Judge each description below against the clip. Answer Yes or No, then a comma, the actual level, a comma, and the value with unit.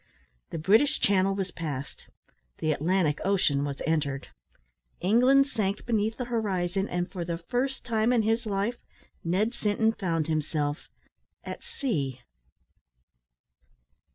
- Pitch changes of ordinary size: No, wide, 5.7 semitones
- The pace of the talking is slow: Yes, slow, 125 wpm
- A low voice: No, high, 195 Hz